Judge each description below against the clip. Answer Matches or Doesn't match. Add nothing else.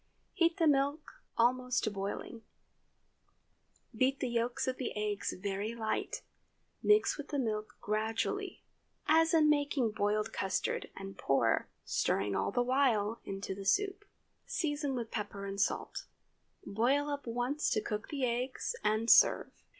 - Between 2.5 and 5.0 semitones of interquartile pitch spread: Doesn't match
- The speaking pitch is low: Doesn't match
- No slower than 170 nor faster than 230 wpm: Doesn't match